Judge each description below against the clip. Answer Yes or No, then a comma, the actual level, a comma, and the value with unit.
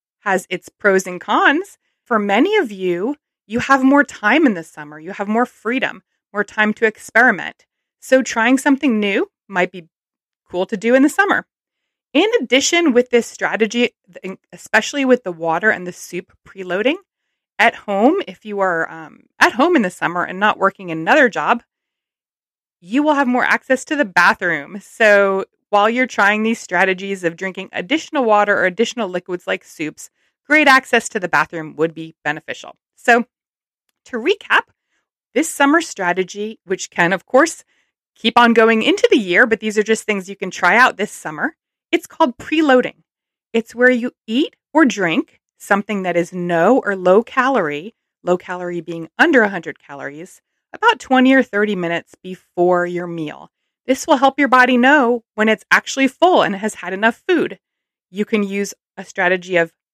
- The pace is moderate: Yes, average, 175 wpm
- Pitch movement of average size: No, wide, 6.1 semitones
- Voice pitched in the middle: No, high, 220 Hz